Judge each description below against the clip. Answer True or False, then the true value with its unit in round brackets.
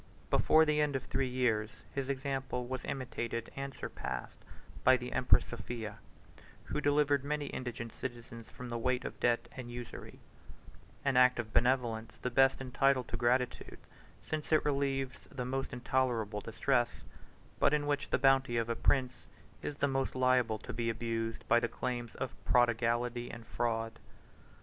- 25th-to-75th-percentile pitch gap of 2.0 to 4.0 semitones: True (2.4 semitones)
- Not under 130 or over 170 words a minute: True (160 wpm)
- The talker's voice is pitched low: True (125 Hz)